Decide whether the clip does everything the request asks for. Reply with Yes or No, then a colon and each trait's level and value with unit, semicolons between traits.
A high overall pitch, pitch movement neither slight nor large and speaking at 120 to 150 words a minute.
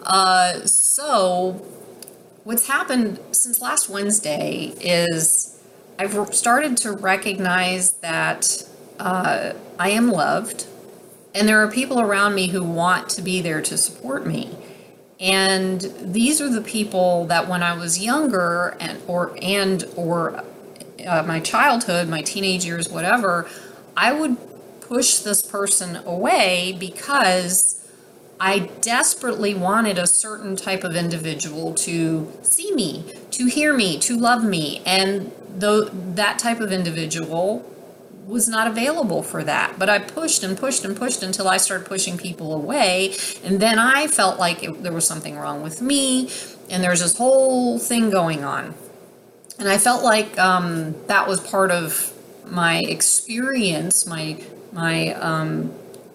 Yes: high, 195 Hz; average, 4.0 semitones; average, 140 wpm